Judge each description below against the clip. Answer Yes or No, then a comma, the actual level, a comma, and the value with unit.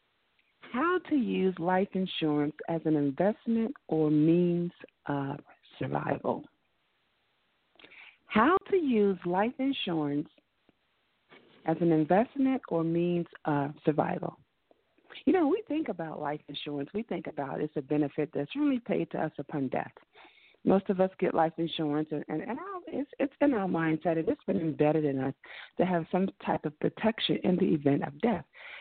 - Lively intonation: Yes, wide, 6.5 semitones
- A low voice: No, medium, 175 Hz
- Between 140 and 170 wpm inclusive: Yes, average, 155 wpm